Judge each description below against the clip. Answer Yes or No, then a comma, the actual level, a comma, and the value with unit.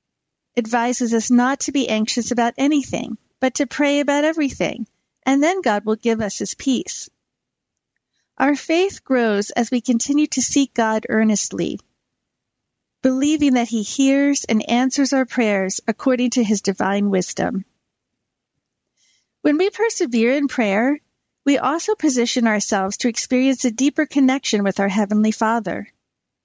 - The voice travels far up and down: No, average, 4.1 semitones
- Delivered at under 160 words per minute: Yes, average, 140 wpm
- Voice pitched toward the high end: Yes, high, 245 Hz